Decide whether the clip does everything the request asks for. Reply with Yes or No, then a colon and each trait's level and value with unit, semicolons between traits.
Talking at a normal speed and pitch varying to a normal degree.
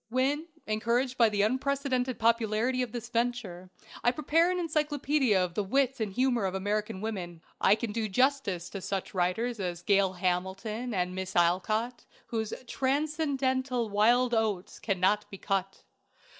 Yes: average, 150 wpm; average, 4.9 semitones